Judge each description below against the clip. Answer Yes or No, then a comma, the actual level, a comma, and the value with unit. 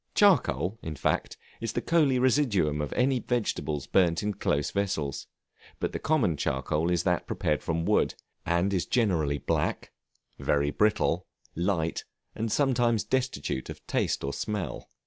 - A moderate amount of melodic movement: No, wide, 7.1 semitones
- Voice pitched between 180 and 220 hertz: No, very low, 90 Hz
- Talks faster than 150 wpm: No, average, 145 wpm